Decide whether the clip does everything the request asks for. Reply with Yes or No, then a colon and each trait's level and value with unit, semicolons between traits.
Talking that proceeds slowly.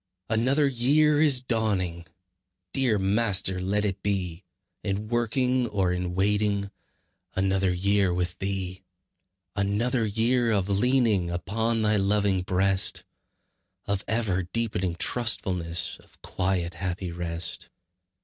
Yes: slow, 110 wpm